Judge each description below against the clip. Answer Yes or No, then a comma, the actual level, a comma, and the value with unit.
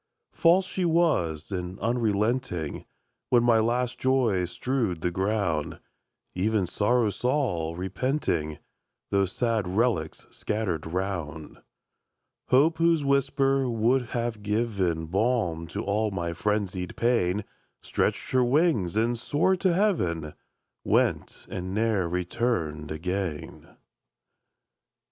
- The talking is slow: Yes, slow, 110 wpm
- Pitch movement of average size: No, wide, 5.9 semitones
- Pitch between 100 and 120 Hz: Yes, low, 105 Hz